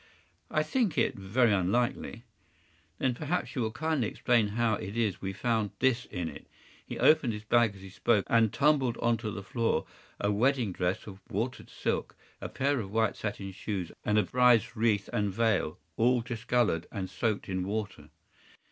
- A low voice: Yes, low, 110 Hz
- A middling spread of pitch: Yes, average, 3.5 semitones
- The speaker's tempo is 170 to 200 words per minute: Yes, average, 185 wpm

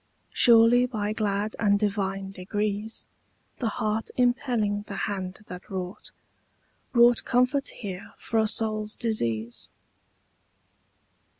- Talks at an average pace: No, slow, 105 wpm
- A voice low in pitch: No, high, 210 Hz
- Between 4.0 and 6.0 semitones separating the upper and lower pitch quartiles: No, narrow, 2.6 semitones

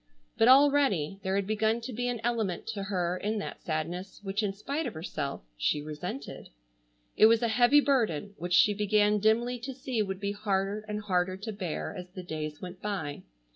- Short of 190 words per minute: No, average, 195 wpm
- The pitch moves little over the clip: No, average, 3.8 semitones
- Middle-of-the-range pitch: No, high, 205 Hz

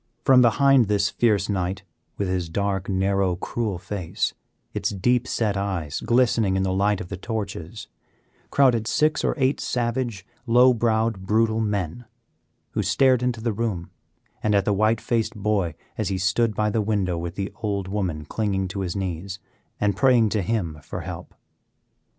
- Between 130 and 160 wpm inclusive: No, average, 170 wpm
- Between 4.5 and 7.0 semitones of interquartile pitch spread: No, average, 3.4 semitones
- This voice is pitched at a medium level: No, low, 105 Hz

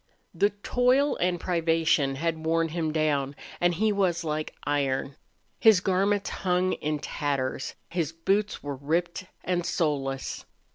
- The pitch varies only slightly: No, average, 3.9 semitones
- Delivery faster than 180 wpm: No, slow, 135 wpm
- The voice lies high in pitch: No, medium, 165 Hz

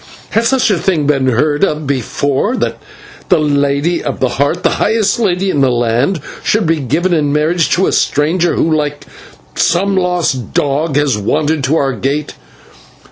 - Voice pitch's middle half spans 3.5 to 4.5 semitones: Yes, average, 4.1 semitones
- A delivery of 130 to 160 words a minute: No, average, 175 wpm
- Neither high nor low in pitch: Yes, medium, 150 Hz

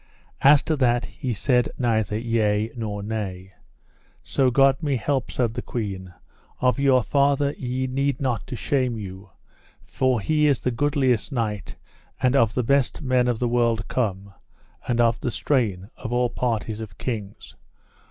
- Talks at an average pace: Yes, average, 160 wpm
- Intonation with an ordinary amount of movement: Yes, average, 3.4 semitones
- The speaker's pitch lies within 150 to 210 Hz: No, low, 120 Hz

